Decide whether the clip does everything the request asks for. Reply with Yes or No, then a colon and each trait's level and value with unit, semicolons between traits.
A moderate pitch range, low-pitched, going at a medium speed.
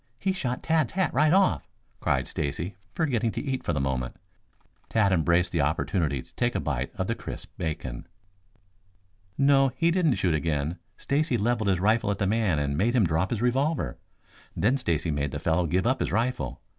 No: wide, 8.5 semitones; low, 100 Hz; average, 190 wpm